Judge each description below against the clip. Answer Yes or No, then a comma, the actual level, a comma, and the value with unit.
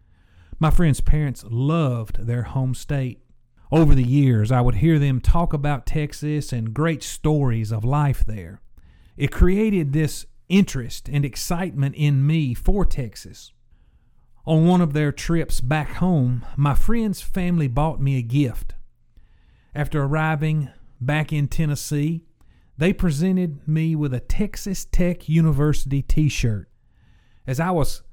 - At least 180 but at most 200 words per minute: No, average, 140 wpm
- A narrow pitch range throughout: No, average, 4.4 semitones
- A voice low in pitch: No, medium, 145 Hz